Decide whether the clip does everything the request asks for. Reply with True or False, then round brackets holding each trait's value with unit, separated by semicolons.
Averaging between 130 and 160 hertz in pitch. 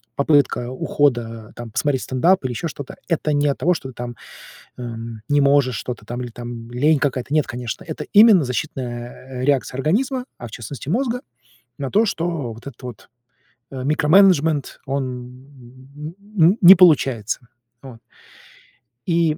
True (135 Hz)